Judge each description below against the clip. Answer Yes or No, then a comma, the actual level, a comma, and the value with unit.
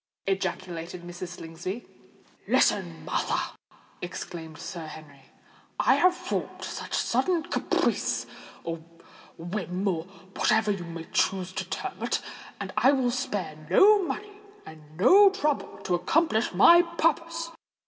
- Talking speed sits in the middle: No, slow, 115 wpm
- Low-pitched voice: No, high, 190 Hz